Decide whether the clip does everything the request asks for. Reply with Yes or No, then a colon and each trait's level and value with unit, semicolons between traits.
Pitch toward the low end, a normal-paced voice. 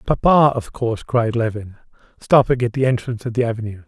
Yes: low, 120 Hz; average, 185 wpm